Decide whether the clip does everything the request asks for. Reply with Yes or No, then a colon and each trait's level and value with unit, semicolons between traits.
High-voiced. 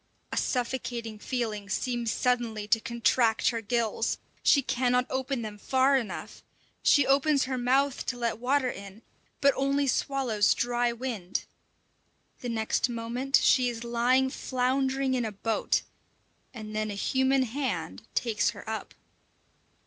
Yes: high, 245 Hz